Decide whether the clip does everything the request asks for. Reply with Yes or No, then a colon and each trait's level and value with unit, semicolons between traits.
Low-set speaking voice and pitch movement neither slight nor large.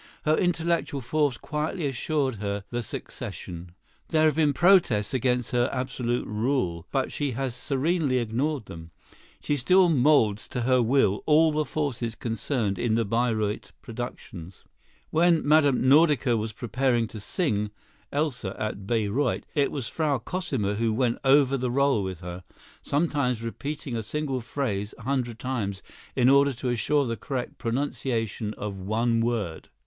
Yes: low, 125 Hz; average, 4.6 semitones